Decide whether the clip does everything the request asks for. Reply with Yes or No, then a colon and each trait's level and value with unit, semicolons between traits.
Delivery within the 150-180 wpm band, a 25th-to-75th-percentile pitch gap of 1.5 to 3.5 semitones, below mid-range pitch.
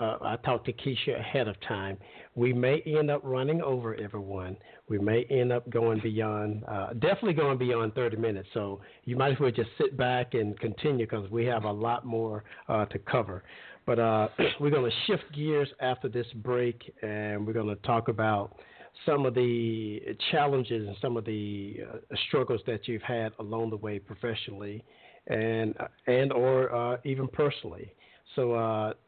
Yes: average, 175 wpm; average, 2.8 semitones; low, 115 Hz